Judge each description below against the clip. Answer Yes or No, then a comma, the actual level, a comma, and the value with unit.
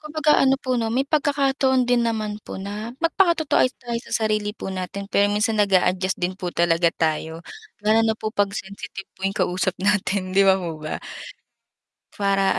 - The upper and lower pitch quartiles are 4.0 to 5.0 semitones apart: Yes, average, 4.3 semitones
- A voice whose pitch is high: Yes, high, 205 Hz